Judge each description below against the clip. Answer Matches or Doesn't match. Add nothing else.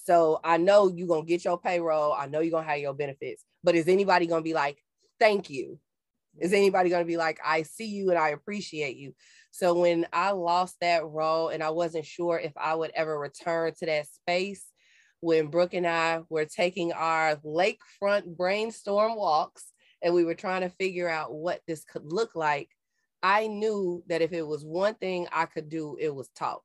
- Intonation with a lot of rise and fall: Doesn't match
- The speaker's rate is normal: Doesn't match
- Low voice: Doesn't match